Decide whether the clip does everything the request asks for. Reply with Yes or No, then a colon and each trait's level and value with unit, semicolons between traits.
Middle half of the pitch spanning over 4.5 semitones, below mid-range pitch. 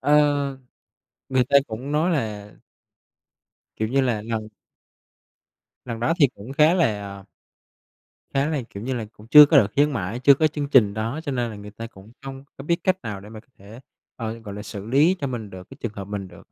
Yes: average, 5.1 semitones; low, 120 Hz